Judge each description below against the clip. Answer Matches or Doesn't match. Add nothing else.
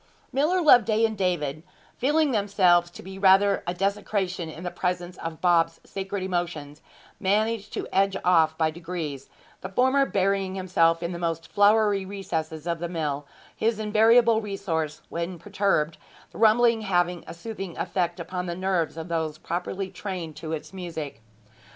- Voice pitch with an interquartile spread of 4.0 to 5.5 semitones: Doesn't match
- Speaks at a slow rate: Doesn't match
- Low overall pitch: Doesn't match